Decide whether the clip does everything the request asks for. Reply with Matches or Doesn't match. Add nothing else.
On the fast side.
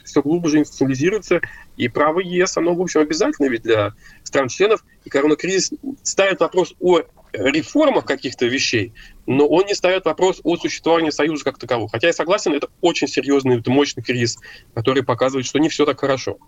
Matches